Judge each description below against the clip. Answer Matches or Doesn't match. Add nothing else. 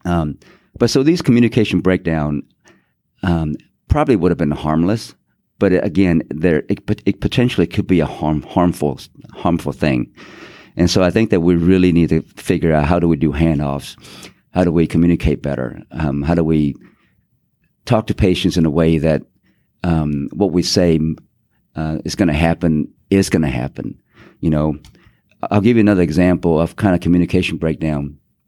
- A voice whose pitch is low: Matches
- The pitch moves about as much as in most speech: Matches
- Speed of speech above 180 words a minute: Doesn't match